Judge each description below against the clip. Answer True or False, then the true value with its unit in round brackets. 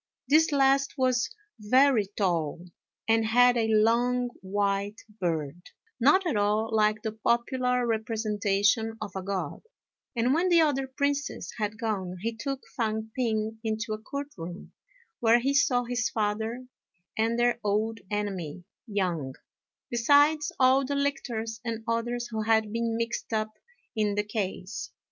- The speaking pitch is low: False (225 Hz)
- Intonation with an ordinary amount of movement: True (3.1 semitones)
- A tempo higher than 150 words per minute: False (145 wpm)